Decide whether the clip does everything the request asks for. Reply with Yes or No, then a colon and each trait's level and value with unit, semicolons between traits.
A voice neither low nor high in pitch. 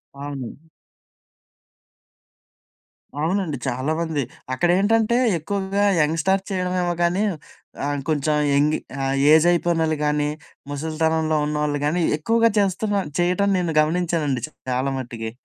Yes: medium, 160 Hz